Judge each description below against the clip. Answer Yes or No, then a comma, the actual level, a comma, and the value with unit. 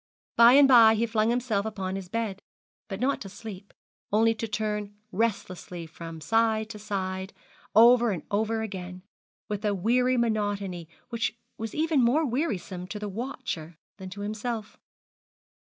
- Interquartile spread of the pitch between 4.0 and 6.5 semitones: No, average, 3.2 semitones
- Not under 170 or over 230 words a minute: No, average, 155 wpm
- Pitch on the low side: No, high, 215 Hz